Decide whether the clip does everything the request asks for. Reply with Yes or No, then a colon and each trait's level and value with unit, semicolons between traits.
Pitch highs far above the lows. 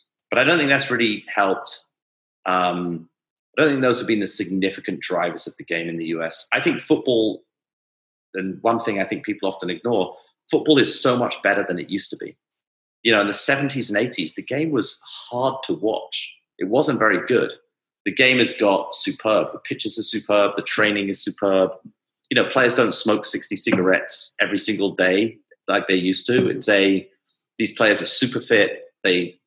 Yes: wide, 6.9 semitones